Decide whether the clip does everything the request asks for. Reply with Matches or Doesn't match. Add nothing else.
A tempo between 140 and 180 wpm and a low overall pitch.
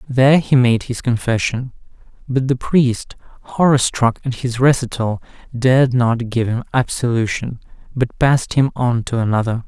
Matches